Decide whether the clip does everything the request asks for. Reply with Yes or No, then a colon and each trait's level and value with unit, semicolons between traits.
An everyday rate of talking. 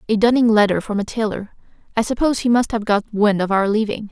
No: fast, 235 wpm